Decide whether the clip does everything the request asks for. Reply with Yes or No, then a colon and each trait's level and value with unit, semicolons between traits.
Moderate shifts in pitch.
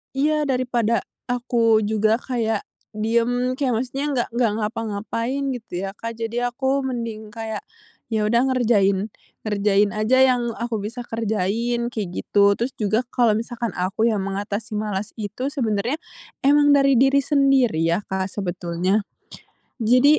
Yes: average, 3.1 semitones